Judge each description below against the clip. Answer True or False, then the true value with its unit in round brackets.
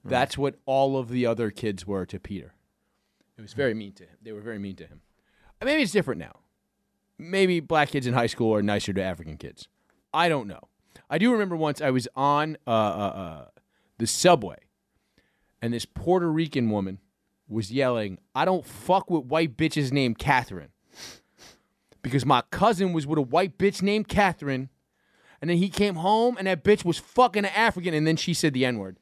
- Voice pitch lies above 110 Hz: True (140 Hz)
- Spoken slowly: False (200 wpm)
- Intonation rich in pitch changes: True (8.6 semitones)